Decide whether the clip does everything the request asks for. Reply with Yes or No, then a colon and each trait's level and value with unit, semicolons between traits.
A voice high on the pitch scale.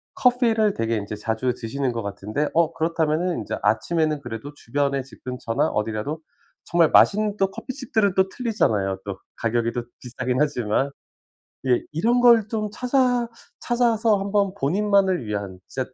No: medium, 155 Hz